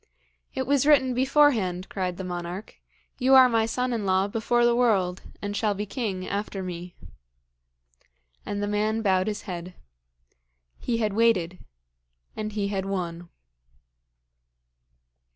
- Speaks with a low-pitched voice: No, high, 205 Hz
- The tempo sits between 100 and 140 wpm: Yes, slow, 135 wpm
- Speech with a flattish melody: No, average, 4.1 semitones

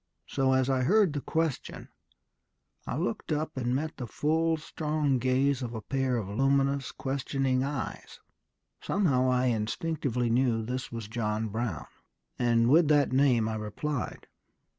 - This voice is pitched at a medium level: No, low, 130 Hz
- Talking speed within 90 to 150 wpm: Yes, average, 145 wpm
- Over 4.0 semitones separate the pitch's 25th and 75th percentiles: No, average, 3.5 semitones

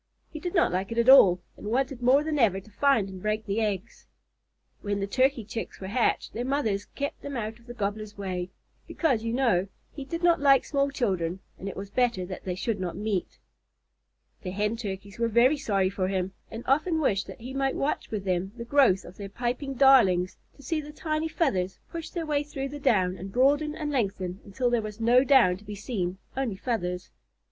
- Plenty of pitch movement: Yes, wide, 5.9 semitones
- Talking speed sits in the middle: No, fast, 215 wpm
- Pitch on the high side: Yes, high, 230 Hz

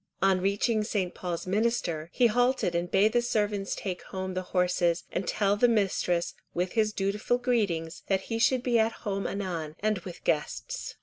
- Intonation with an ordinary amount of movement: Yes, average, 3.5 semitones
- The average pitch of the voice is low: No, high, 195 Hz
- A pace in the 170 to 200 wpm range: Yes, average, 180 wpm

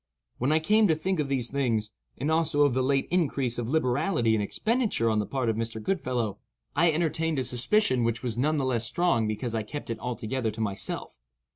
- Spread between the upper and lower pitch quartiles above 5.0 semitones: Yes, wide, 5.5 semitones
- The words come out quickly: Yes, fast, 215 wpm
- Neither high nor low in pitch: No, low, 130 Hz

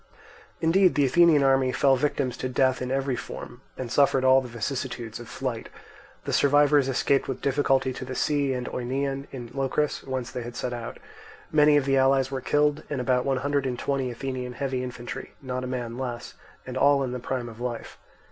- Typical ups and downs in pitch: No, narrow, 1.9 semitones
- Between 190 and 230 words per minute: Yes, average, 200 wpm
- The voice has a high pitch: No, low, 130 Hz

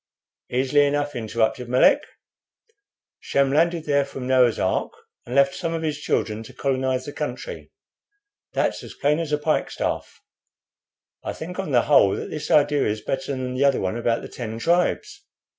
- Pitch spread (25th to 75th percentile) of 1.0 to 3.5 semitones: Yes, average, 3.1 semitones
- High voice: No, medium, 140 Hz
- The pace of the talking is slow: No, average, 170 wpm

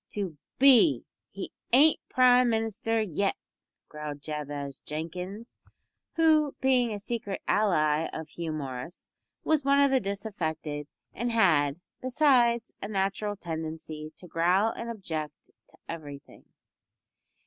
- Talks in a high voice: Yes, high, 195 Hz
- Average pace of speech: No, slow, 120 wpm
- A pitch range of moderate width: No, wide, 7.1 semitones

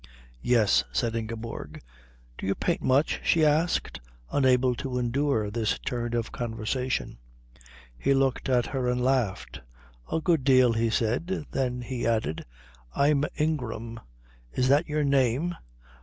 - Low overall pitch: Yes, low, 125 Hz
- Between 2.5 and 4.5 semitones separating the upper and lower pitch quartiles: Yes, average, 3.3 semitones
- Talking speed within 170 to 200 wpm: No, average, 140 wpm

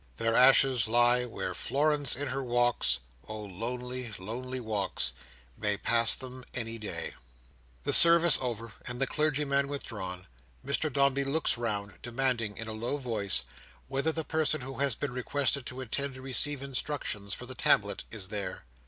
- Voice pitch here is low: Yes, low, 125 Hz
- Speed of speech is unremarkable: Yes, average, 155 wpm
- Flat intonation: No, average, 4.1 semitones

